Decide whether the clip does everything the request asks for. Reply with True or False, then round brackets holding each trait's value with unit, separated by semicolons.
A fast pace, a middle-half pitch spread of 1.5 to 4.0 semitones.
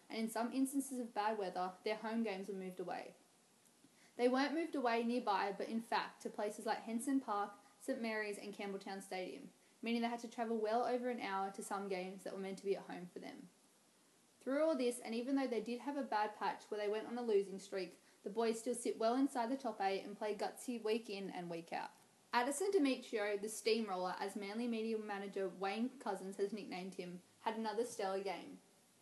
True (215 wpm; 3.3 semitones)